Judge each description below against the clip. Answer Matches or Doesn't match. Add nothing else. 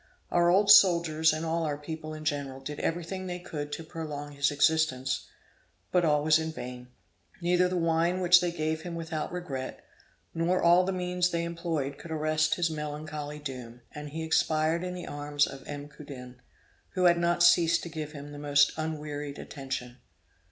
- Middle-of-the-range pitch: Matches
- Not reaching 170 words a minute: Doesn't match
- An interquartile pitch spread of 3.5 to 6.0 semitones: Doesn't match